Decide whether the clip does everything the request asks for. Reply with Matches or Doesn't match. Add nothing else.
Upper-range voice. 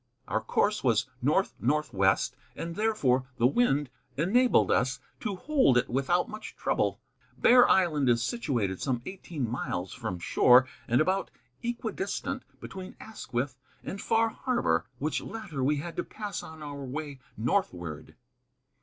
Doesn't match